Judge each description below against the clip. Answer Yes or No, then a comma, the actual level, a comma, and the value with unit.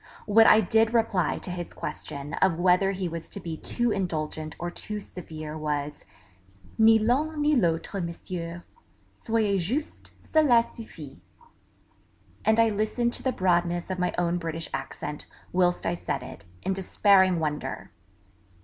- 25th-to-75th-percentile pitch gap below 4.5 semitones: No, average, 4.9 semitones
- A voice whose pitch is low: No, medium, 180 Hz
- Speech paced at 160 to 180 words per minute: No, average, 150 wpm